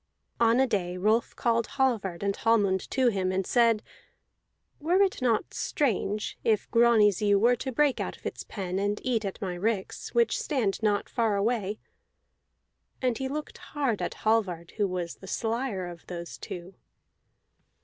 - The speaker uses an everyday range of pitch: Yes, average, 3.9 semitones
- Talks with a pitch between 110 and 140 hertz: No, high, 215 Hz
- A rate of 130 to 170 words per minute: Yes, average, 165 wpm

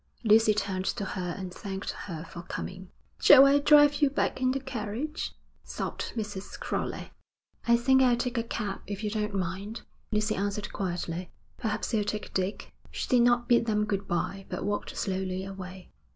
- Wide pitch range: No, average, 3.8 semitones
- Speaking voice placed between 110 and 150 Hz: No, high, 210 Hz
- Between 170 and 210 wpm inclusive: Yes, average, 180 wpm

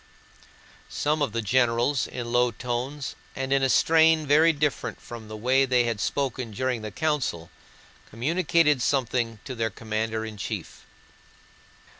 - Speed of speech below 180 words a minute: Yes, average, 145 wpm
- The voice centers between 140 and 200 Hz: No, low, 125 Hz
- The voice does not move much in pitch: No, average, 4.1 semitones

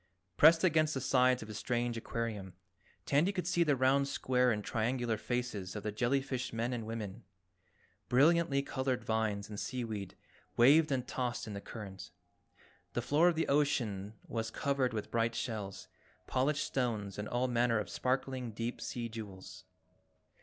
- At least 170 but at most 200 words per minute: No, average, 160 wpm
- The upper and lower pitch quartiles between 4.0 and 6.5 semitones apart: No, average, 3.6 semitones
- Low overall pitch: Yes, low, 120 Hz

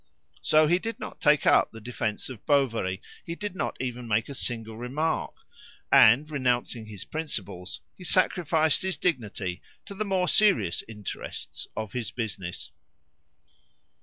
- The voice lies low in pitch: Yes, low, 125 Hz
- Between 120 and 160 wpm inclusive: Yes, average, 145 wpm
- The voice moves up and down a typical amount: No, wide, 6.7 semitones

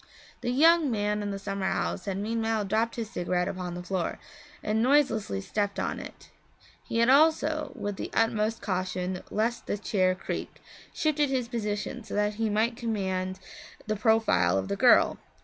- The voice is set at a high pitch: Yes, high, 210 Hz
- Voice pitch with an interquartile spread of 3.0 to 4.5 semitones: Yes, average, 3.6 semitones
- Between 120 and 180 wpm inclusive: Yes, average, 170 wpm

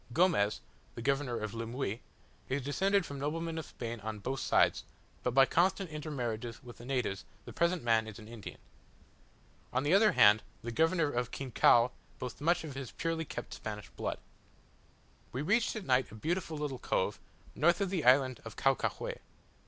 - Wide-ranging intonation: Yes, wide, 5.7 semitones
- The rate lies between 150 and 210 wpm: Yes, average, 175 wpm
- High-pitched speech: No, low, 135 Hz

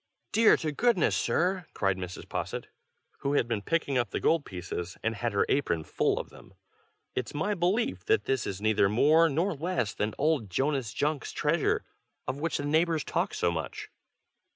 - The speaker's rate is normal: Yes, average, 180 wpm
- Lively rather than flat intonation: Yes, wide, 7.7 semitones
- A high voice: No, medium, 140 Hz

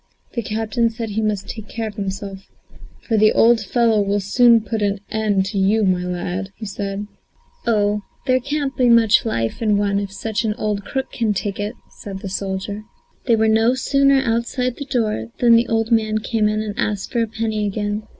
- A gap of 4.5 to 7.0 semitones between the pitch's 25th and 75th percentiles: No, narrow, 2.4 semitones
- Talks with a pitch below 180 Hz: No, high, 215 Hz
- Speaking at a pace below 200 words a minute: No, fast, 205 wpm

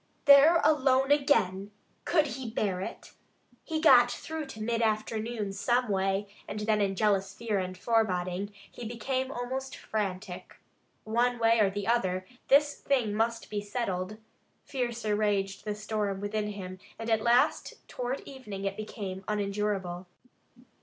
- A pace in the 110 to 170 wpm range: Yes, average, 145 wpm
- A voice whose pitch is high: Yes, high, 215 Hz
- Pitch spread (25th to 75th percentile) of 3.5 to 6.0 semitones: Yes, average, 3.8 semitones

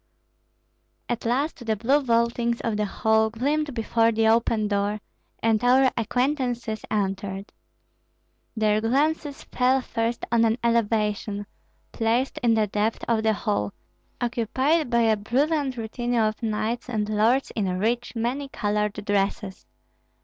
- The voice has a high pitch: Yes, high, 230 Hz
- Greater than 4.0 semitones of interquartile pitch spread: No, narrow, 2.4 semitones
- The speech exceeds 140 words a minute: No, slow, 135 wpm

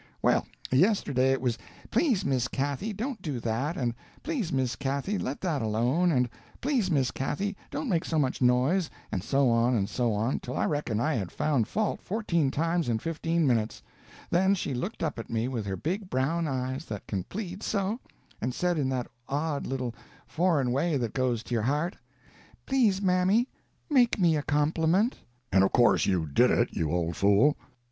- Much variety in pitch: Yes, wide, 6.5 semitones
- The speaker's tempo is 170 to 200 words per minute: Yes, average, 185 wpm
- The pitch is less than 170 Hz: Yes, medium, 140 Hz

